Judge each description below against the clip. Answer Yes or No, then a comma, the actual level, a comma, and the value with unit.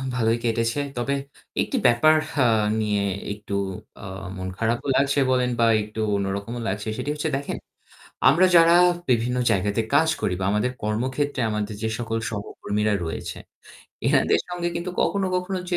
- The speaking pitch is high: No, low, 115 Hz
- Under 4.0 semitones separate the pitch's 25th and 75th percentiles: No, average, 5.1 semitones